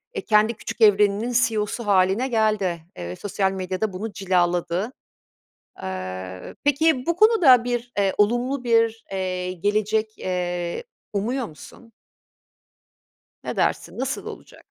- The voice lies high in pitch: Yes, high, 210 Hz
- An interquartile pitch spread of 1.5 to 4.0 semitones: No, average, 4.5 semitones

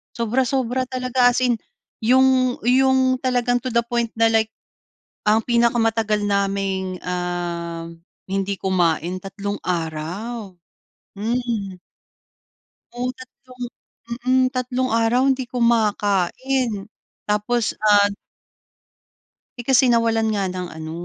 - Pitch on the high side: Yes, high, 225 Hz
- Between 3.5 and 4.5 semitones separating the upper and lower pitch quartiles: Yes, average, 4.2 semitones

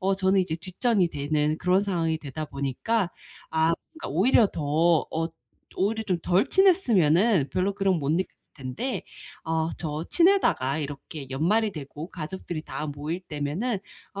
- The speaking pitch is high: No, medium, 170 Hz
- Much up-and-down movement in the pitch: No, average, 4.5 semitones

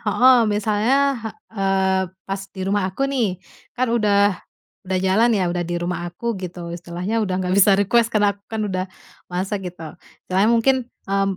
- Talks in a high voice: Yes, high, 195 Hz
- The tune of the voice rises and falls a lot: No, average, 2.8 semitones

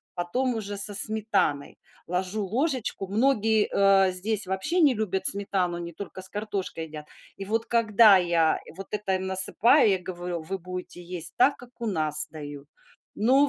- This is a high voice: Yes, high, 195 Hz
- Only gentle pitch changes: No, average, 3.6 semitones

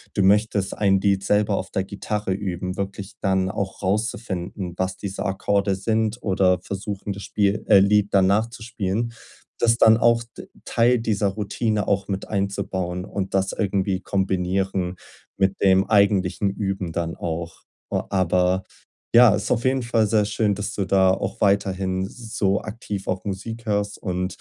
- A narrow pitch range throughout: Yes, narrow, 1.9 semitones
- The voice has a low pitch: Yes, low, 100 Hz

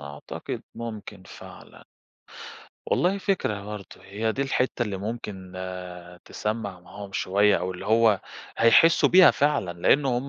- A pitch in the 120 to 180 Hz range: No, low, 105 Hz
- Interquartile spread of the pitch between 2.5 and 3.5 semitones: No, average, 4.3 semitones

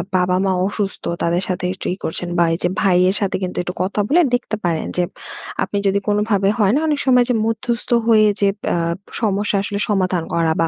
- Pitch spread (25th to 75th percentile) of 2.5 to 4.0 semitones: Yes, average, 3.0 semitones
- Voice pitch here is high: Yes, high, 195 Hz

